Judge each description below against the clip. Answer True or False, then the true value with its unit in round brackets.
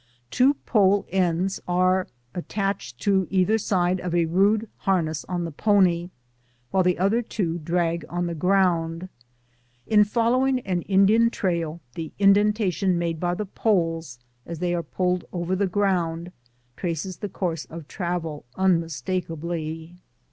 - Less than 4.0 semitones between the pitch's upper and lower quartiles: True (2.7 semitones)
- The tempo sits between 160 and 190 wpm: False (140 wpm)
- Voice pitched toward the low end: False (180 Hz)